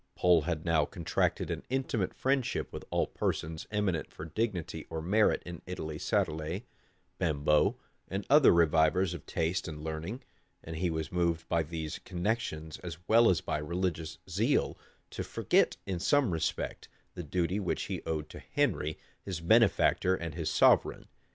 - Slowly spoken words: No, average, 160 wpm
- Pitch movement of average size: Yes, average, 3.3 semitones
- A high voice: No, very low, 85 Hz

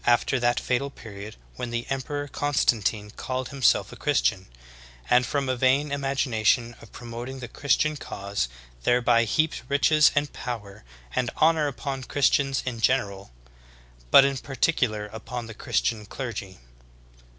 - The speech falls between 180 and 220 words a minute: No, average, 140 wpm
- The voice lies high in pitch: No, low, 125 Hz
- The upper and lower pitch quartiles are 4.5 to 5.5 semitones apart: No, average, 3.5 semitones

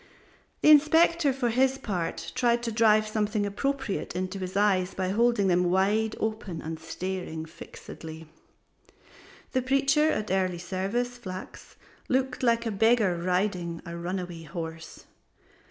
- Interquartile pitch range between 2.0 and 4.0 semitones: No, average, 5.0 semitones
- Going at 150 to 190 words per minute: No, average, 140 wpm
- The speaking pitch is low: No, high, 200 Hz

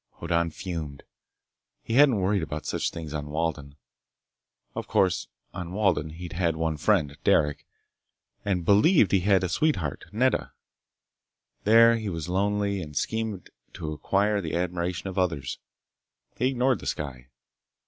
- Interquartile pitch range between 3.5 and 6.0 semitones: Yes, average, 4.6 semitones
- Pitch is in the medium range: No, very low, 90 Hz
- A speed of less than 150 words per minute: Yes, average, 140 wpm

